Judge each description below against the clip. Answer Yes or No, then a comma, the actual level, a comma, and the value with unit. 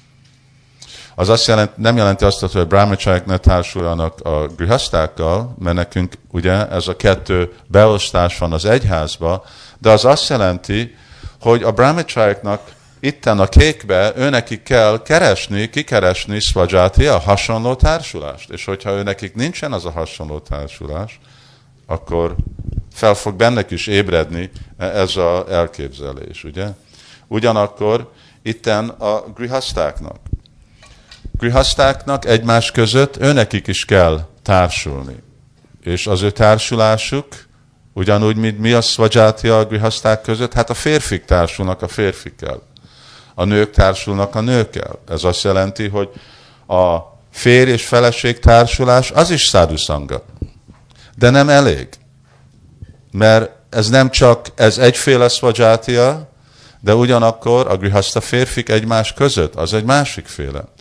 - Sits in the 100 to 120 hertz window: Yes, low, 110 Hz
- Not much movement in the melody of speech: No, average, 4.7 semitones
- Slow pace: No, average, 125 wpm